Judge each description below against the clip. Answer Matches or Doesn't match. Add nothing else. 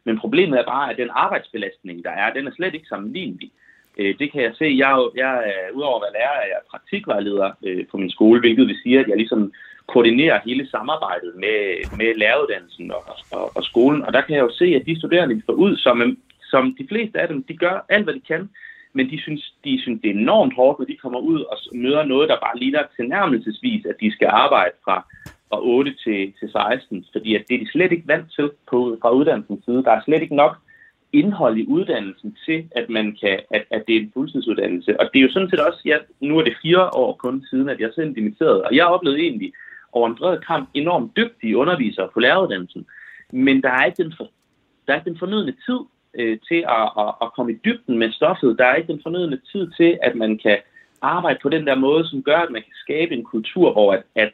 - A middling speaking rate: Doesn't match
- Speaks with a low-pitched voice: Doesn't match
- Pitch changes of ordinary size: Doesn't match